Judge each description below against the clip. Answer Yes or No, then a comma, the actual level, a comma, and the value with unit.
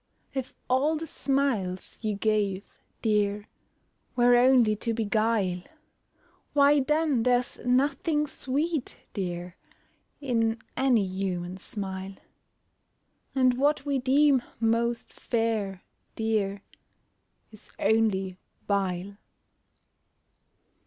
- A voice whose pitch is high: Yes, high, 225 Hz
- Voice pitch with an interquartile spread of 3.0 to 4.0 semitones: No, average, 5.0 semitones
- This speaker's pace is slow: Yes, slow, 90 wpm